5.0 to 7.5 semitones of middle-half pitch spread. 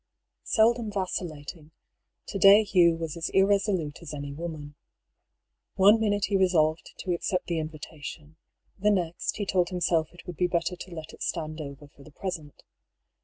No: average, 3.7 semitones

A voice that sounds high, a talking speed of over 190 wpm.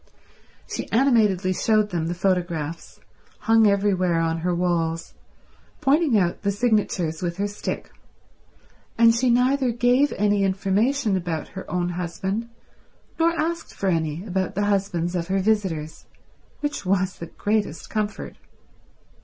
No: high, 195 Hz; slow, 135 wpm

